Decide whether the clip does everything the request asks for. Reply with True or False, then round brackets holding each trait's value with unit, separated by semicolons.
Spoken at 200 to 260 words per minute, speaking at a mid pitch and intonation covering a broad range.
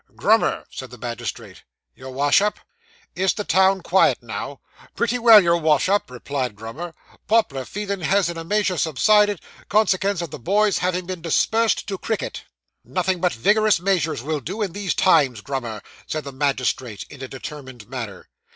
False (165 wpm; 170 Hz; 6.9 semitones)